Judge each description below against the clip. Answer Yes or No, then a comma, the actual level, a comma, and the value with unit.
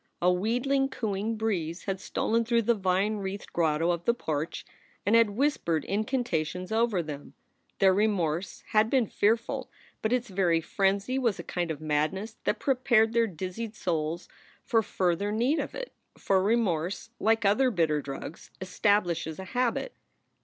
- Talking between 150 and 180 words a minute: Yes, average, 160 wpm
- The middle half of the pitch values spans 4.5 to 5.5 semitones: Yes, average, 4.9 semitones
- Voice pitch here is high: Yes, high, 200 Hz